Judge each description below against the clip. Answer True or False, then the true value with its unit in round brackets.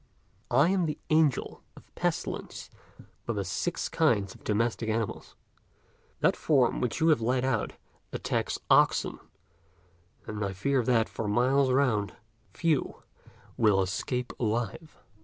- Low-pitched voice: True (120 Hz)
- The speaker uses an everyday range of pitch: True (4.5 semitones)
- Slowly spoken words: True (130 wpm)